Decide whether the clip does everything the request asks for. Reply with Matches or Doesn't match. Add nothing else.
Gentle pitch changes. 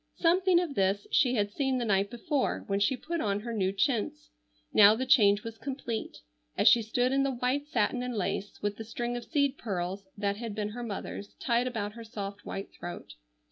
Doesn't match